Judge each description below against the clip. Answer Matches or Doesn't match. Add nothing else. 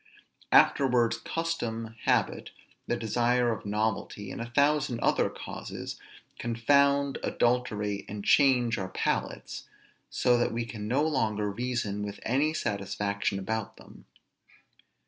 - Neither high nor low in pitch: Doesn't match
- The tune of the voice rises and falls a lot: Doesn't match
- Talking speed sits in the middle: Doesn't match